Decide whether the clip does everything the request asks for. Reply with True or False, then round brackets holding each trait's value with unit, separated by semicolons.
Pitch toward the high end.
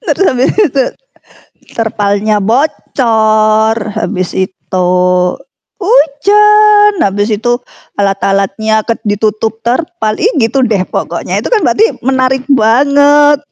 True (230 Hz)